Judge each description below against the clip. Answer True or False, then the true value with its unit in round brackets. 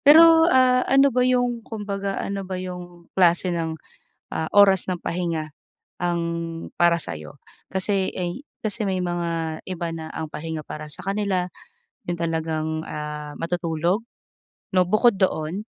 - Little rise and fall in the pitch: False (3.6 semitones)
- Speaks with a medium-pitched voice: True (180 Hz)